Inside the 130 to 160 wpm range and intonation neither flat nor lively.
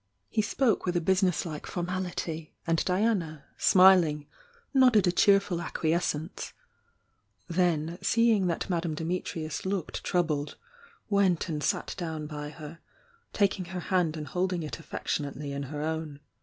Yes: average, 140 wpm; average, 3.3 semitones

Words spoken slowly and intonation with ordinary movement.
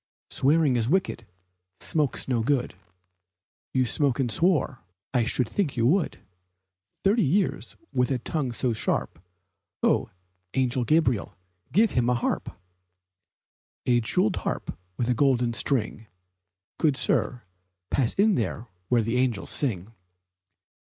Yes: slow, 125 wpm; average, 4.1 semitones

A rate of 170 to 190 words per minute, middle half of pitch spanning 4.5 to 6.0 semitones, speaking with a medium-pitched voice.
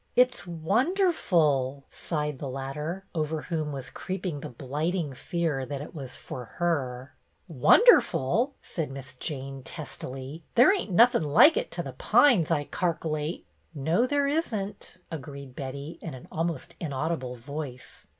Yes: average, 175 wpm; average, 4.8 semitones; medium, 155 Hz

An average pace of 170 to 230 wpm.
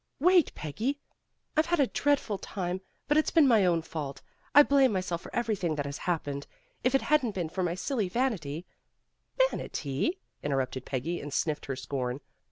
Yes: average, 175 wpm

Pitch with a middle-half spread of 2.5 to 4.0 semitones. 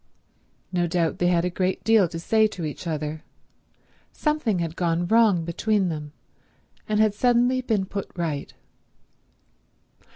No: average, 4.6 semitones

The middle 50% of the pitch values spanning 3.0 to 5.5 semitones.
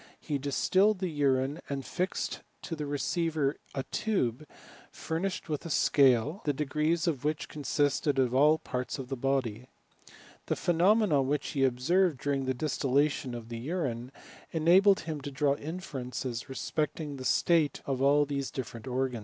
Yes: average, 3.4 semitones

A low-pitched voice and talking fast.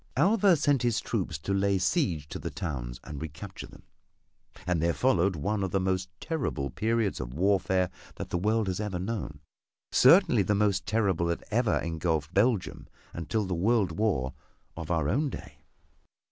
No: very low, 95 Hz; average, 170 wpm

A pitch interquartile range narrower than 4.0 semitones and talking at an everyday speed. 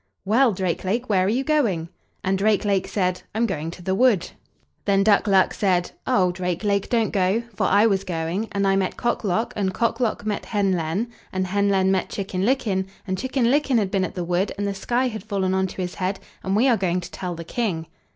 No: average, 2.9 semitones; fast, 235 wpm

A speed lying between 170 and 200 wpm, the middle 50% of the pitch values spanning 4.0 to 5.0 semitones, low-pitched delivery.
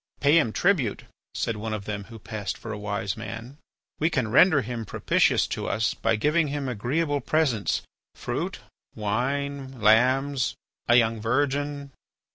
No: average, 150 wpm; average, 4.5 semitones; low, 125 Hz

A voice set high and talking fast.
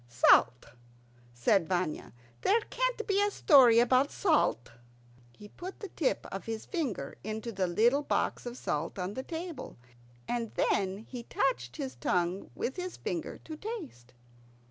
No: high, 235 Hz; average, 150 wpm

